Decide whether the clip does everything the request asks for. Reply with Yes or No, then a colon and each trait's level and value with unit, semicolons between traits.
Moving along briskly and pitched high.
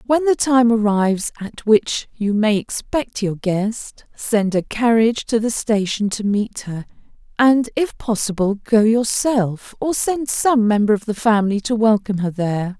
No: average, 170 wpm; high, 220 Hz